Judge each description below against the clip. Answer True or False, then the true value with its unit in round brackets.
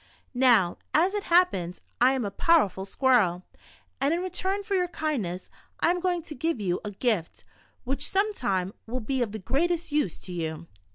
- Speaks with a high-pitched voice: True (260 Hz)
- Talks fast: False (190 wpm)